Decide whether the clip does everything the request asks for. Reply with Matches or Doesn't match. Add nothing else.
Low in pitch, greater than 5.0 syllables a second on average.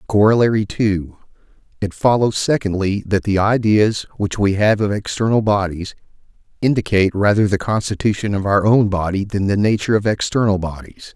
Matches